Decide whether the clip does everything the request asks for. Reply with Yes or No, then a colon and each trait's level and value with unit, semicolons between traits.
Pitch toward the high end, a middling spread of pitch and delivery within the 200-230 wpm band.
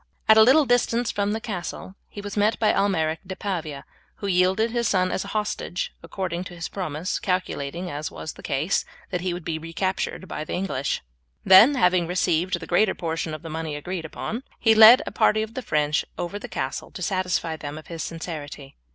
No: medium, 180 Hz; average, 4.0 semitones; fast, 205 wpm